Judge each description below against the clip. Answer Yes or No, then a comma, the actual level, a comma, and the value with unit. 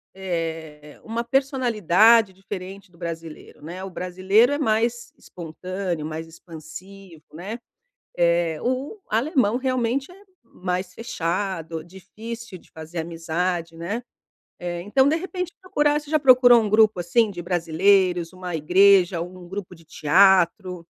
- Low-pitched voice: No, medium, 185 Hz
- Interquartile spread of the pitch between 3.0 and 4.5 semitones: No, average, 5.3 semitones